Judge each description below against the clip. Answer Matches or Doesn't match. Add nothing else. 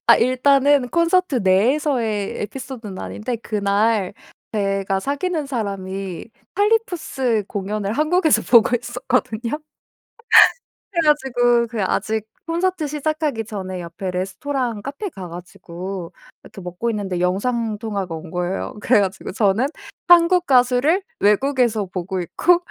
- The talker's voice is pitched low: Doesn't match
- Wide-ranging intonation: Matches